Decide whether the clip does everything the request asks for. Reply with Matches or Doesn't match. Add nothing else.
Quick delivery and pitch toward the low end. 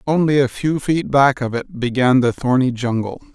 Doesn't match